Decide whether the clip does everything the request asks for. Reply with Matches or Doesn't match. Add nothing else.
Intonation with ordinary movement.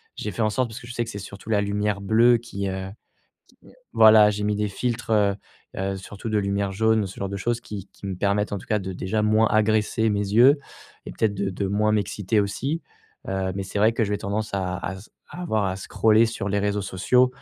Doesn't match